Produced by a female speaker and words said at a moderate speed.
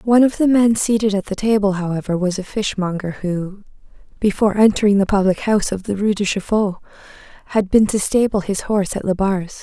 Yes: female; average, 195 wpm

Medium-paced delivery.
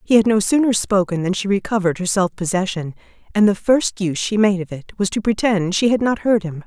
No: fast, 245 wpm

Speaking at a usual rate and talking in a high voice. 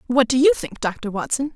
No: fast, 230 wpm; very high, 255 Hz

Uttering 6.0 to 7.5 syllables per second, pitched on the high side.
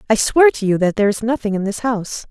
Yes: 6.7 syllables/s; high, 220 Hz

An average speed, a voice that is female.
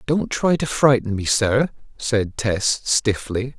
No: average, 150 wpm; male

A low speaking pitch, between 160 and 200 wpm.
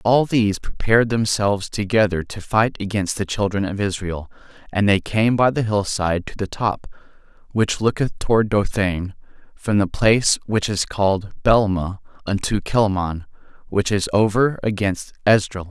No: low, 105 Hz; average, 150 wpm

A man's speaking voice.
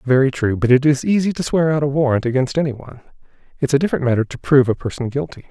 Yes: male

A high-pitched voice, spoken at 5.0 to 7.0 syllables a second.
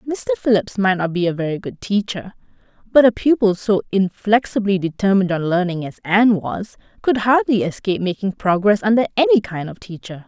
Yes: high, 205 Hz; 5.5 syllables/s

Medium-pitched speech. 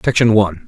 No: low, 105 Hz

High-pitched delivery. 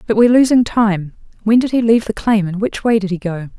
Yes: high, 210 Hz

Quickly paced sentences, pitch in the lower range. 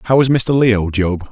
Yes: fast, 230 wpm; low, 110 Hz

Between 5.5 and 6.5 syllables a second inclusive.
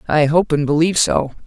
Yes: 5.8 syllables/s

